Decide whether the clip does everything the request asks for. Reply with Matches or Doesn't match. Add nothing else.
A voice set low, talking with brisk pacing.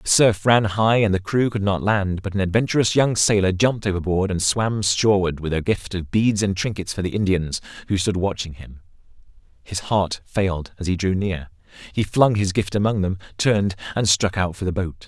Matches